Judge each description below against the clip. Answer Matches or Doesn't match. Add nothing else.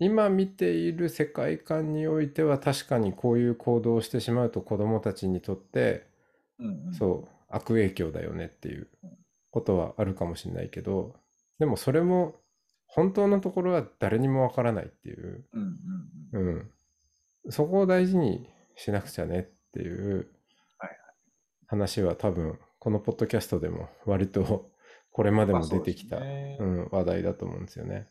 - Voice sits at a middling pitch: Doesn't match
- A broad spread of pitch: Matches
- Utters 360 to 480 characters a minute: Doesn't match